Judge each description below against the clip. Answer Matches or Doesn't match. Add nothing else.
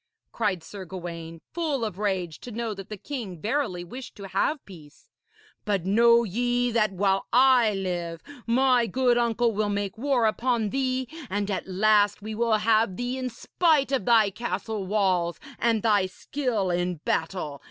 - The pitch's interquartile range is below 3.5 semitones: Doesn't match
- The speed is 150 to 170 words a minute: Matches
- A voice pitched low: Doesn't match